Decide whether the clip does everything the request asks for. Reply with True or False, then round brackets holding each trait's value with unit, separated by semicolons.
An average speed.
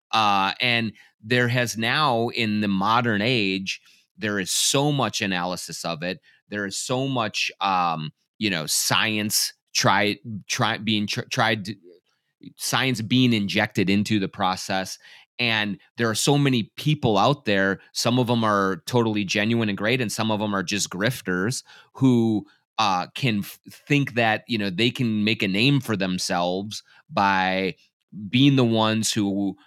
True (160 wpm)